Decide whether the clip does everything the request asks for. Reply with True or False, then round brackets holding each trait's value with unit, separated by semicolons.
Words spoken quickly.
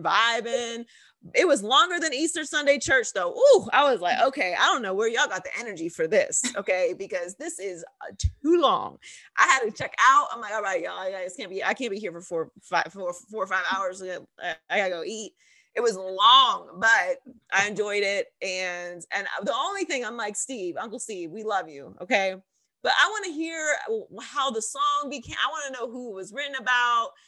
True (220 wpm)